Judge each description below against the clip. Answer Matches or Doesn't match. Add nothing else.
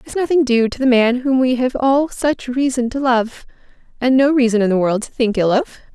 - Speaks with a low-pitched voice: Doesn't match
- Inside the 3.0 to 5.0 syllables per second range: Doesn't match